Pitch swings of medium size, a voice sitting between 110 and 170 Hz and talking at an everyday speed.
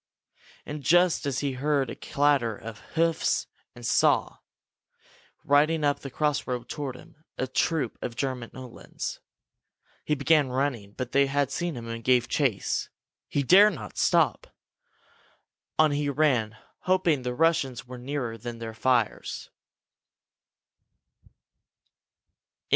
No: average, 3.5 semitones; low, 135 Hz; slow, 130 wpm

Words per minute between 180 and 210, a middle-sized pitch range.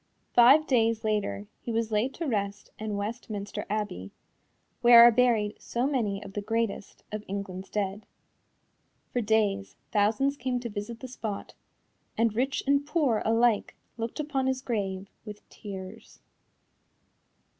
No: average, 140 wpm; average, 3.1 semitones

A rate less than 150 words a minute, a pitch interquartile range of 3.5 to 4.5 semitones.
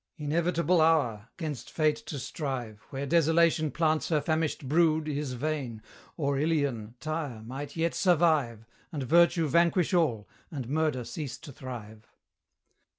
Yes: slow, 135 wpm; average, 4.0 semitones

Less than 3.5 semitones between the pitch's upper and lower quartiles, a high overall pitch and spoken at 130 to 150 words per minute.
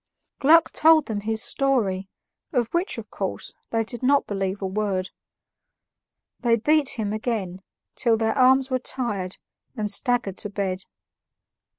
No: average, 4.6 semitones; high, 225 Hz; average, 145 wpm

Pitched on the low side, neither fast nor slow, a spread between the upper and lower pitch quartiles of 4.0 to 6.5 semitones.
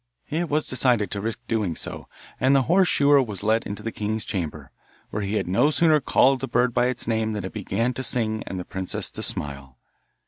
No: low, 110 Hz; fast, 220 wpm; average, 4.5 semitones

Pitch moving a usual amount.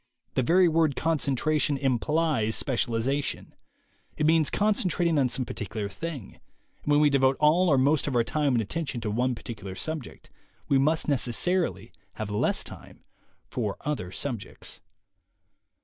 Yes: average, 5.0 semitones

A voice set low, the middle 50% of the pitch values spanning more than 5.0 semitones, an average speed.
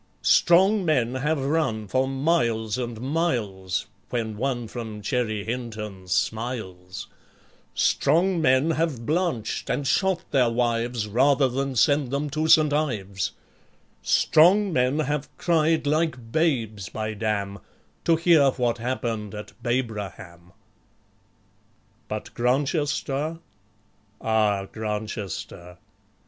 No: low, 125 Hz; wide, 5.6 semitones; slow, 105 wpm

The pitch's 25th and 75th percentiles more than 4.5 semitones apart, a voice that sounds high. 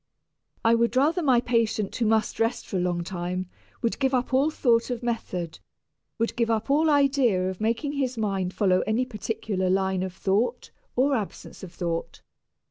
Yes: average, 5.1 semitones; high, 225 Hz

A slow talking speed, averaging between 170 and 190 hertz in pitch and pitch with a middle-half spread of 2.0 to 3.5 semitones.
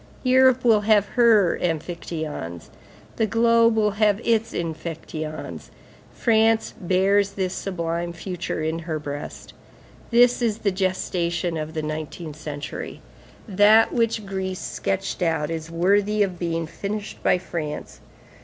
No: slow, 125 wpm; medium, 185 Hz; average, 4.5 semitones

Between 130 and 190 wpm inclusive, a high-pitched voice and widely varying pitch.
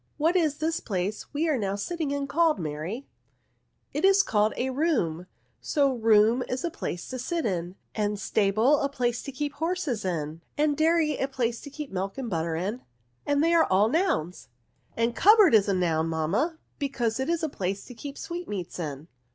No: fast, 205 wpm; very high, 250 Hz; wide, 7.8 semitones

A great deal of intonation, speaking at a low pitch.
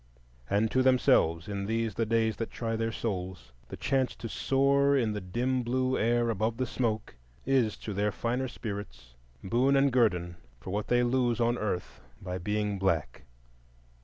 No: average, 3.8 semitones; low, 115 Hz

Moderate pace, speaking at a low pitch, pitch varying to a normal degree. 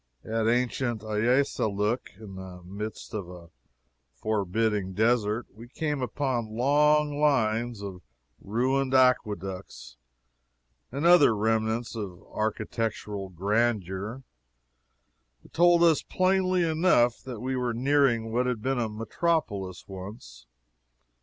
No: slow, 105 wpm; low, 115 Hz; average, 4.2 semitones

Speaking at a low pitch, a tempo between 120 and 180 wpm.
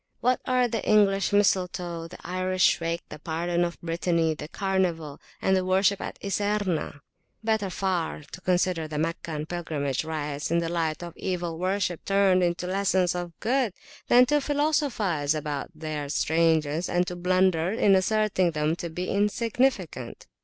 No: medium, 180 Hz; average, 155 wpm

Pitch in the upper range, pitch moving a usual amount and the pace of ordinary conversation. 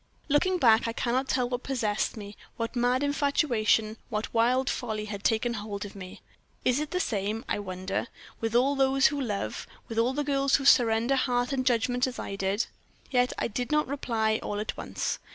Yes: high, 240 Hz; average, 3.7 semitones; average, 190 wpm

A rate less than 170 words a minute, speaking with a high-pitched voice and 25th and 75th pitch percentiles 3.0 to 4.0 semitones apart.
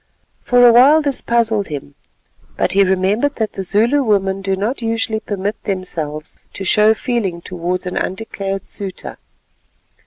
Yes: average, 150 wpm; high, 205 Hz; average, 3.3 semitones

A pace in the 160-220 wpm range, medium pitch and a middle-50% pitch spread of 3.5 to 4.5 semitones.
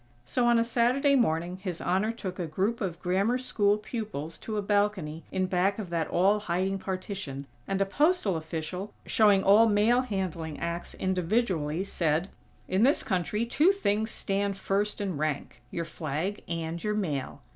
No: average, 170 wpm; high, 195 Hz; average, 3.9 semitones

